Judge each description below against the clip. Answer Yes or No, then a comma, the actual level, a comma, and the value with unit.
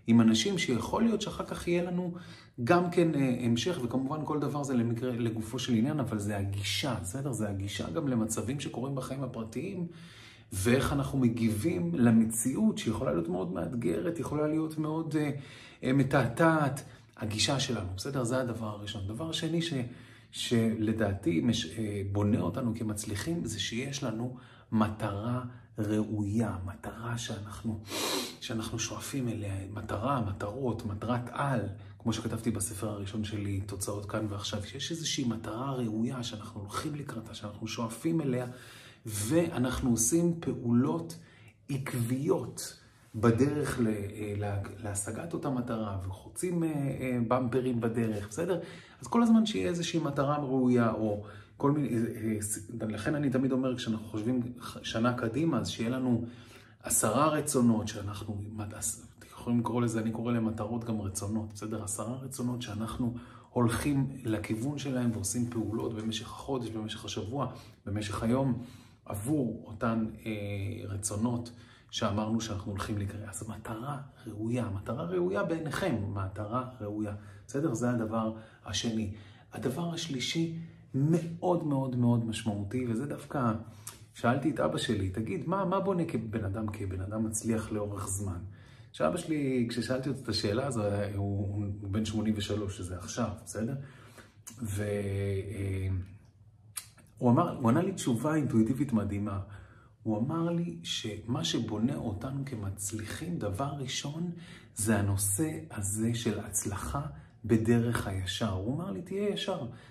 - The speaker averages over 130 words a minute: No, average, 125 wpm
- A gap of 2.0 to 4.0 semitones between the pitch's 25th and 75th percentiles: Yes, average, 3.7 semitones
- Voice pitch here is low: Yes, low, 115 Hz